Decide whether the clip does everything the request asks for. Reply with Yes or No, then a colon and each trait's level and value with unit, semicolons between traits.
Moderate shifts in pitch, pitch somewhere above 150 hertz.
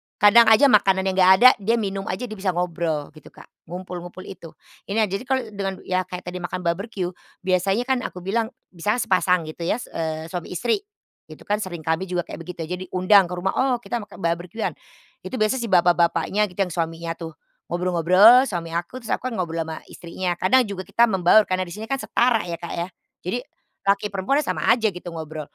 Yes: average, 3.7 semitones; medium, 185 Hz